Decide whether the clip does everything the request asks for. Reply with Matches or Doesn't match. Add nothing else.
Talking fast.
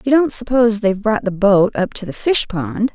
Matches